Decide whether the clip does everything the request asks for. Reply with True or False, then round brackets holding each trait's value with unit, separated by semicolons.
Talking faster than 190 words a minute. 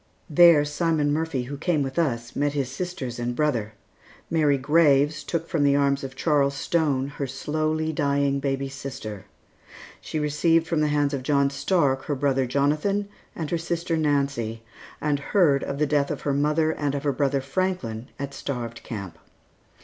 False (170 wpm)